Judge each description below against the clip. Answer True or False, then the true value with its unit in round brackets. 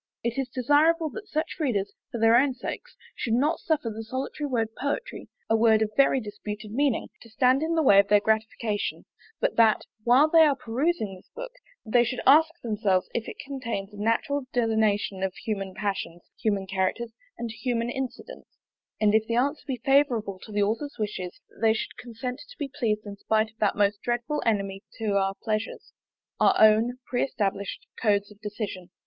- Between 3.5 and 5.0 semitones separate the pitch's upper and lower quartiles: True (4.1 semitones)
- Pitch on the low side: False (225 Hz)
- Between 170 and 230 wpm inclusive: True (190 wpm)